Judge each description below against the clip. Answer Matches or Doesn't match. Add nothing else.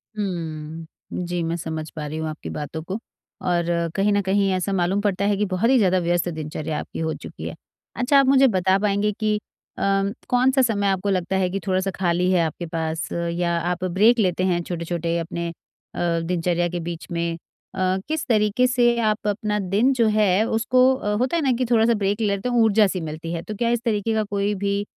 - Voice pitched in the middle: Doesn't match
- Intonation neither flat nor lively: Matches